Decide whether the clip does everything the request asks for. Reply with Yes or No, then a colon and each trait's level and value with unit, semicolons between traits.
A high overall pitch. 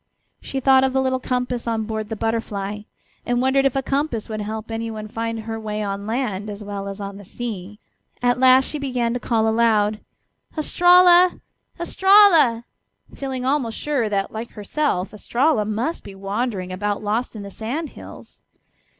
Yes: high, 230 Hz